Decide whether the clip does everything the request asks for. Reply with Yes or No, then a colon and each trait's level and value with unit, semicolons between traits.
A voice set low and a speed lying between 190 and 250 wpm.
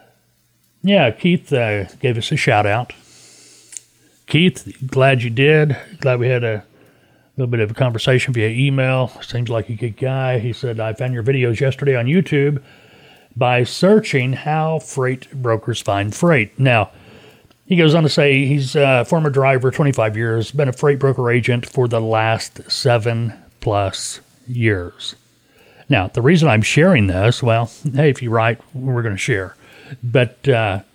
No: low, 130 Hz; average, 165 wpm